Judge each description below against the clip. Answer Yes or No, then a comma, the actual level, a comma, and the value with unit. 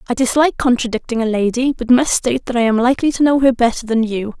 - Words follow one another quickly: Yes, fast, 245 wpm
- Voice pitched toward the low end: No, high, 245 Hz